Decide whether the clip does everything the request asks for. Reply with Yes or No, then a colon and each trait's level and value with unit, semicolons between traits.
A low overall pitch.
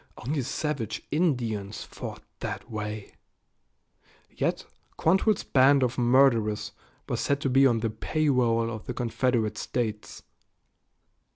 Yes: low, 120 Hz